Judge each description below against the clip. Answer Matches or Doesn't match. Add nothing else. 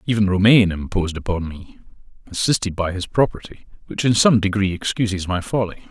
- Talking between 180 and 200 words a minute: Doesn't match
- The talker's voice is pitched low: Matches